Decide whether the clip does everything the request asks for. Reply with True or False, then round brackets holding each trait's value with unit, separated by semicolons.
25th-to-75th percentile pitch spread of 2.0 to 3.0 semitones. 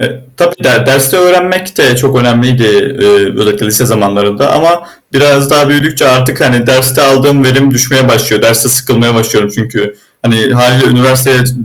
True (2.7 semitones)